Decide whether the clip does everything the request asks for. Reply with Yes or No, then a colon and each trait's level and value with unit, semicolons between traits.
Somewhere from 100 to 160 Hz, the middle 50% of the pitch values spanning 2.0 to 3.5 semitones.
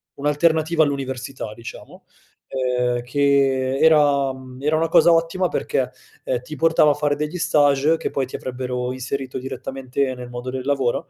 Yes: low, 135 Hz; narrow, 2.6 semitones